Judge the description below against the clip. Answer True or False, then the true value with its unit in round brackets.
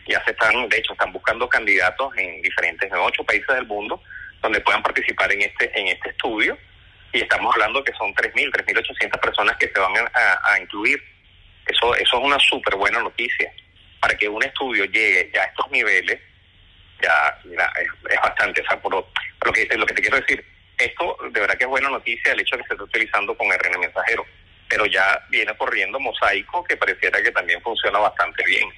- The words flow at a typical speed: False (200 wpm)